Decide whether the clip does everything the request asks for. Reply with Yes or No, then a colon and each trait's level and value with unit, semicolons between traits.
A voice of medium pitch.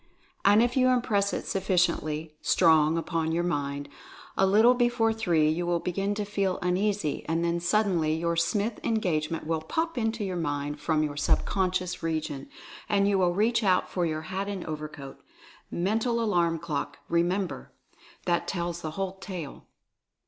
Yes: medium, 175 Hz